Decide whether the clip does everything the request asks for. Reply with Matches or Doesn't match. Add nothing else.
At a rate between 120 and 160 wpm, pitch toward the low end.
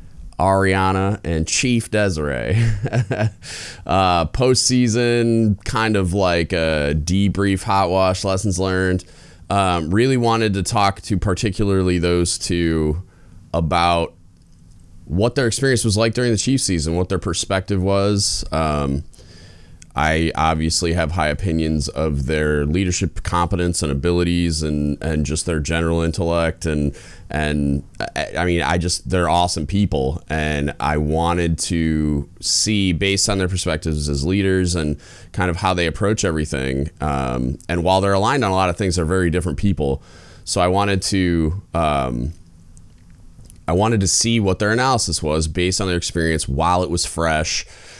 Matches